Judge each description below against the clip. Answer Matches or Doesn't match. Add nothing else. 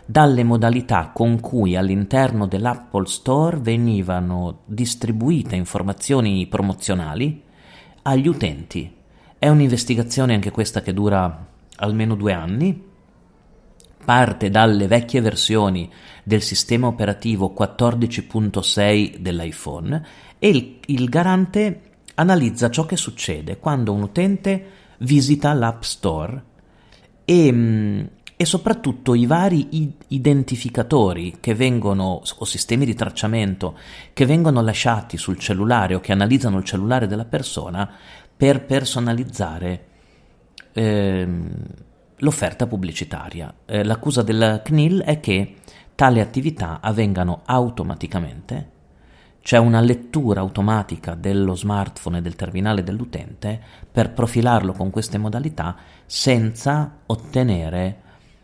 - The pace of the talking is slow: Matches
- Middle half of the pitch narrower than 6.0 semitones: Matches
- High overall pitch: Doesn't match